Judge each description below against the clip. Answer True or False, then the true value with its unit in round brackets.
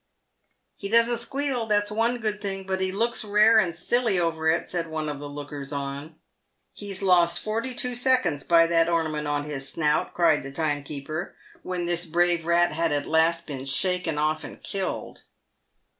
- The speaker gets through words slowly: False (185 wpm)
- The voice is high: False (170 Hz)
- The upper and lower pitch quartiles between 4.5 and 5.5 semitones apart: True (5.1 semitones)